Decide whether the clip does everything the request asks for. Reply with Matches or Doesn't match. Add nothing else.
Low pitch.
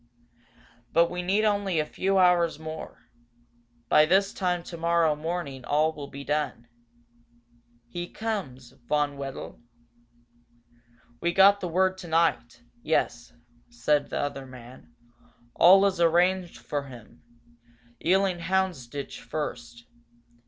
Doesn't match